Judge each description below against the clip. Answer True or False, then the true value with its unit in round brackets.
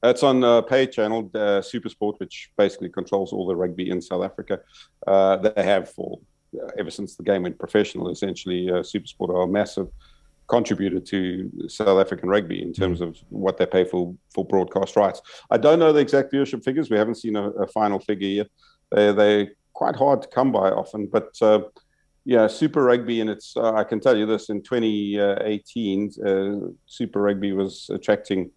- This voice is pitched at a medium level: False (105 Hz)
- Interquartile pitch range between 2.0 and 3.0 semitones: True (2.7 semitones)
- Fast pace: False (195 wpm)